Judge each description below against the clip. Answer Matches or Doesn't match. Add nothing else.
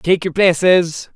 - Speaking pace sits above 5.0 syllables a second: Doesn't match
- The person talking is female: Doesn't match